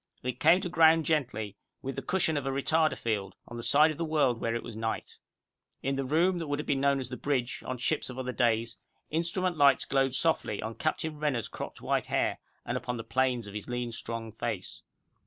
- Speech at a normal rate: No, fast, 225 wpm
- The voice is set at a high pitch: No, low, 135 Hz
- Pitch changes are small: No, average, 4.8 semitones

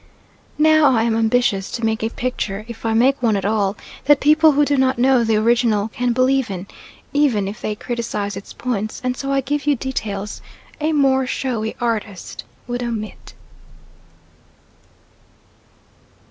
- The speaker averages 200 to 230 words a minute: No, average, 155 wpm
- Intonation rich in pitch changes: No, average, 3.6 semitones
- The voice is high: Yes, high, 240 Hz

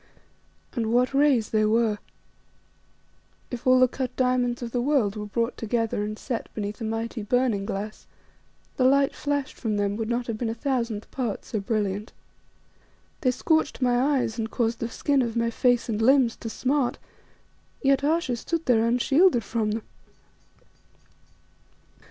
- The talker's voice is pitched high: Yes, high, 235 Hz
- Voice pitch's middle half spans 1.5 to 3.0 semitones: Yes, average, 2.7 semitones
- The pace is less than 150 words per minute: No, average, 160 wpm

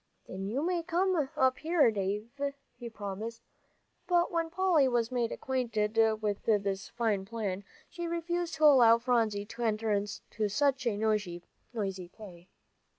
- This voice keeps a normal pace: Yes, average, 145 wpm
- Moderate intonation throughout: No, wide, 5.8 semitones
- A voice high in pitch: Yes, high, 230 Hz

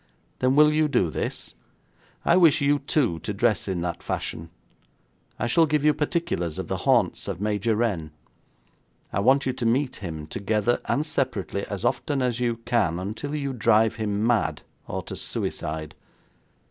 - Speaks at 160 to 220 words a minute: Yes, average, 170 wpm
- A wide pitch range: Yes, wide, 6.2 semitones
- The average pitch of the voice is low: Yes, low, 115 Hz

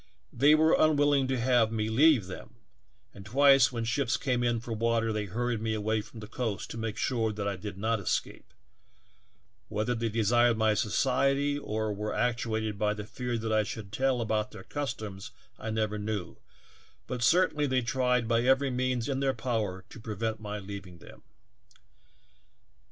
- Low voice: Yes, low, 115 Hz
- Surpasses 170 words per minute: Yes, average, 180 wpm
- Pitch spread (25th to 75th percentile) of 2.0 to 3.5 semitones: Yes, average, 3.0 semitones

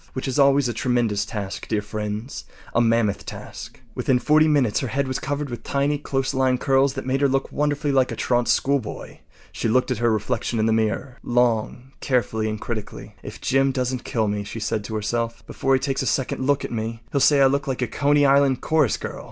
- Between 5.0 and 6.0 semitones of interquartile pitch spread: No, average, 3.5 semitones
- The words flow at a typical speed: No, fast, 215 wpm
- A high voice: No, low, 130 Hz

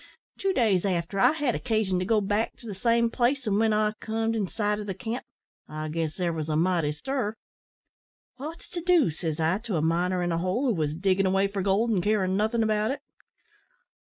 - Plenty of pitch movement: No, average, 4.1 semitones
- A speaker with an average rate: No, fast, 220 wpm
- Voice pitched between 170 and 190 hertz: No, high, 205 Hz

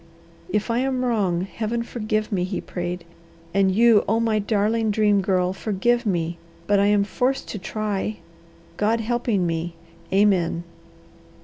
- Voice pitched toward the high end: Yes, high, 210 Hz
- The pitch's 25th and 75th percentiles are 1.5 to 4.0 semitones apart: Yes, average, 3.3 semitones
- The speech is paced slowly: No, average, 145 wpm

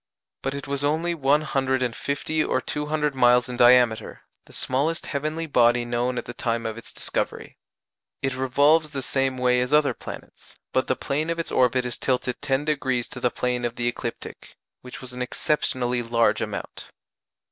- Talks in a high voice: No, low, 130 Hz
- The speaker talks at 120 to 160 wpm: No, average, 185 wpm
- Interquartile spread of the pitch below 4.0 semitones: Yes, average, 2.8 semitones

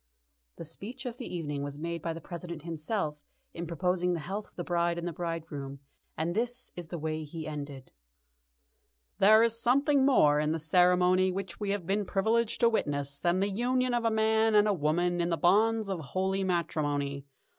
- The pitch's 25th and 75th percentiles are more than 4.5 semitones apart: Yes, average, 5.1 semitones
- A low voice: No, medium, 175 Hz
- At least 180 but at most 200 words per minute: Yes, average, 190 wpm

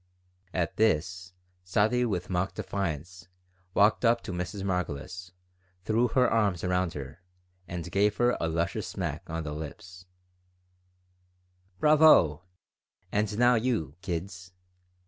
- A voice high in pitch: No, very low, 90 Hz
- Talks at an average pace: No, slow, 120 wpm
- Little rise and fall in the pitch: No, average, 3.7 semitones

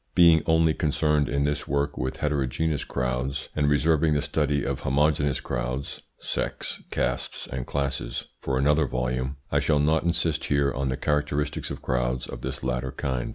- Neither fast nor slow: Yes, average, 165 wpm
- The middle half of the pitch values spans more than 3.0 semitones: No, narrow, 2.5 semitones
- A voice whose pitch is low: Yes, very low, 70 Hz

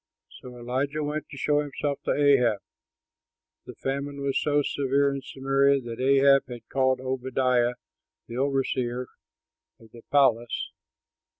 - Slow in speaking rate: Yes, slow, 130 wpm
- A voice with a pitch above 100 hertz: Yes, low, 135 Hz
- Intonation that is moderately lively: No, narrow, 2.0 semitones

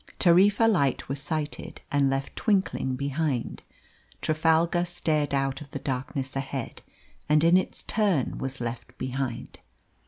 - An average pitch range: Yes, average, 3.9 semitones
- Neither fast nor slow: No, slow, 130 wpm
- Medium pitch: Yes, medium, 145 Hz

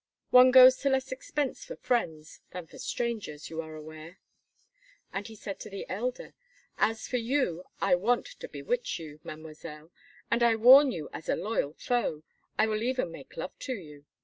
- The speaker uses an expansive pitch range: Yes, wide, 7.9 semitones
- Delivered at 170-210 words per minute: Yes, average, 180 wpm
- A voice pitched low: No, high, 215 Hz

